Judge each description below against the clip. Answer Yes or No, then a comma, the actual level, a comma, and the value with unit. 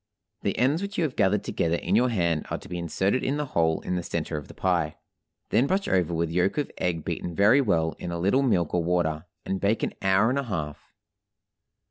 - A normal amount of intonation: No, wide, 6.6 semitones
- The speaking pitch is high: No, very low, 90 Hz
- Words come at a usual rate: No, fast, 230 wpm